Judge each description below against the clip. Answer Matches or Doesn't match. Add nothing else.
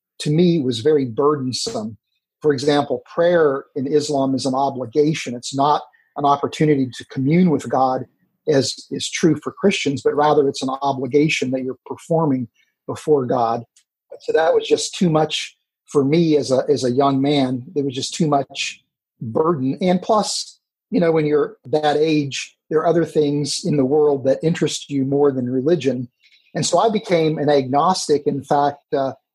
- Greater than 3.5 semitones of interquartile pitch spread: Doesn't match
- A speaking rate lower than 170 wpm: Doesn't match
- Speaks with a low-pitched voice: Doesn't match